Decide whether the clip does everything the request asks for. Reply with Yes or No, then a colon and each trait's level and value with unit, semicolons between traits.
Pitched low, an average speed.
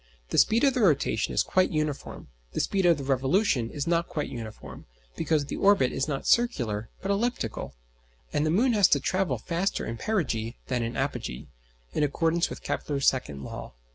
No: medium, 150 Hz; average, 185 wpm